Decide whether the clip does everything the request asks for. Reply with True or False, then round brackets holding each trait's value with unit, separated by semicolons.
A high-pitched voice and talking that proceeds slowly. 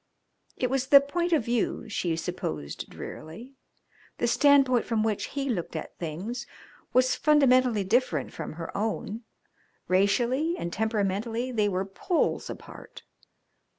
True (230 Hz; 130 wpm)